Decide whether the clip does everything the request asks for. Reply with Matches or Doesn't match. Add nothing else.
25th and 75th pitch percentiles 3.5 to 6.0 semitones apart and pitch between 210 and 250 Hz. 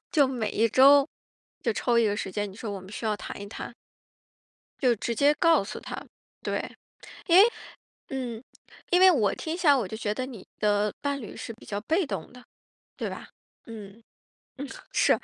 Matches